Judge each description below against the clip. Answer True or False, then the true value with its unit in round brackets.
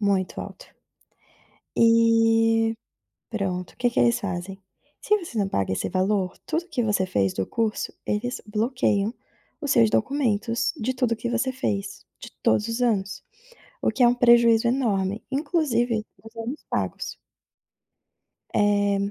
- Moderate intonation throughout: True (3.3 semitones)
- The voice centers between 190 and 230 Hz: True (225 Hz)